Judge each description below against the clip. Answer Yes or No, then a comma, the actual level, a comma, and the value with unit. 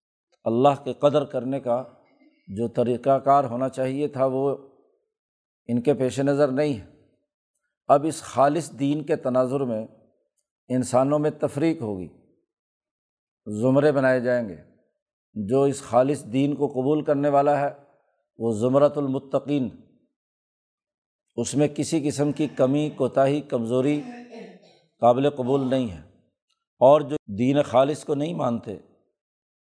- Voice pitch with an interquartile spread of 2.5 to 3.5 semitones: Yes, average, 2.8 semitones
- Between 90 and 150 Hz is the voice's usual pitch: Yes, medium, 140 Hz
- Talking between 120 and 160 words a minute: Yes, average, 130 wpm